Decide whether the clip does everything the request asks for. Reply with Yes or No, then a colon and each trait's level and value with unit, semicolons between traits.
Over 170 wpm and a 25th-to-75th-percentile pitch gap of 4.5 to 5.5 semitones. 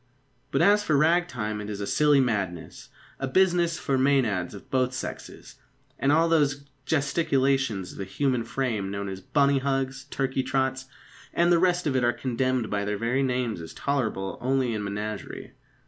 Yes: average, 180 wpm; average, 4.9 semitones